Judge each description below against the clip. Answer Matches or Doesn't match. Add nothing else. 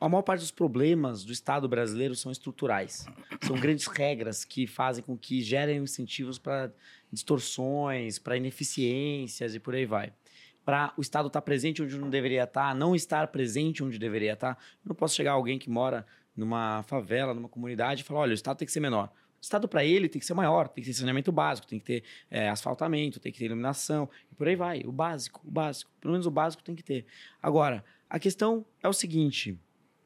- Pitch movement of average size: Matches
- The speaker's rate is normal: Doesn't match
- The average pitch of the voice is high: Doesn't match